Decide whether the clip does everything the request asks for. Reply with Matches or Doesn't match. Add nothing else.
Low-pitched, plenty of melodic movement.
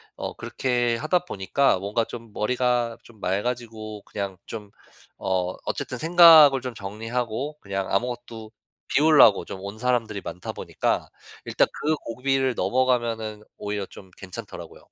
Doesn't match